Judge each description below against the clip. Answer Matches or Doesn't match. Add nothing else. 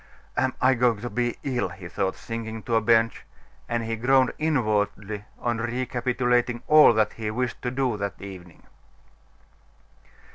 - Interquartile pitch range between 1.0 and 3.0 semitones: Matches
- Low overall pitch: Matches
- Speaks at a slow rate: Doesn't match